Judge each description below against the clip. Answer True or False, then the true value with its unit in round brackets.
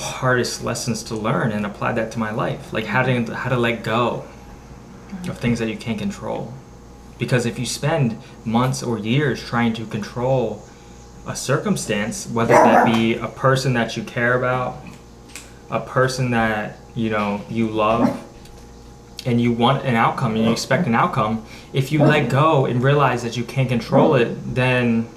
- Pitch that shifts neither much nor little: False (2.2 semitones)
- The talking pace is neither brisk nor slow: True (175 wpm)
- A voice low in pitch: True (120 Hz)